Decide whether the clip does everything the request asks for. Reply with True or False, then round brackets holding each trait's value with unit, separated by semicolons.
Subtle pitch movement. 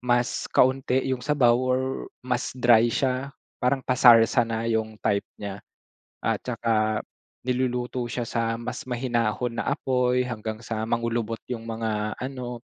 True (1.9 semitones)